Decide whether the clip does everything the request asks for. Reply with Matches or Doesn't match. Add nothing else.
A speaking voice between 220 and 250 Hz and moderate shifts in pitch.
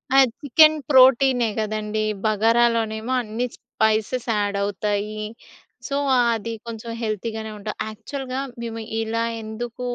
Doesn't match